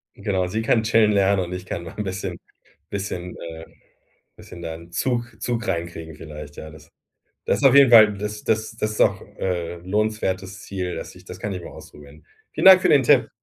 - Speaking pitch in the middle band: No, very low, 95 Hz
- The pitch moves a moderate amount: Yes, average, 3.9 semitones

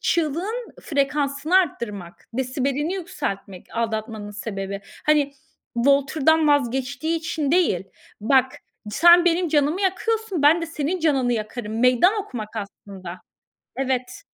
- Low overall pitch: No, very high, 280 Hz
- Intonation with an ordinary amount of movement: No, wide, 6.2 semitones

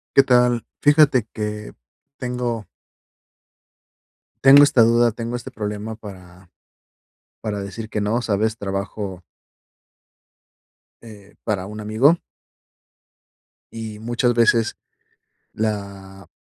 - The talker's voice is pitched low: Yes, low, 110 Hz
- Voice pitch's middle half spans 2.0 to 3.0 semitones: Yes, average, 2.7 semitones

